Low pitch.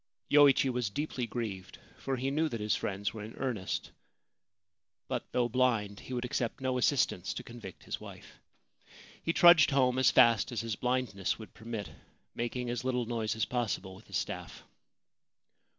Yes: low, 120 Hz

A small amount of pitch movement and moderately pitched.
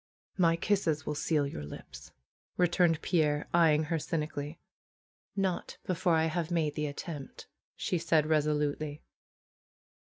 Yes: narrow, 2.2 semitones; medium, 160 Hz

